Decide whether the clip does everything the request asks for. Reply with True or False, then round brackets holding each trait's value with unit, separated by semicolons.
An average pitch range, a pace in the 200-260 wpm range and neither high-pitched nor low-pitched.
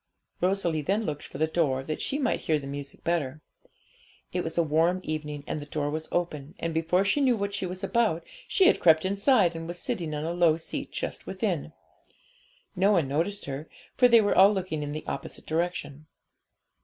True (4.2 semitones; 205 wpm; 165 Hz)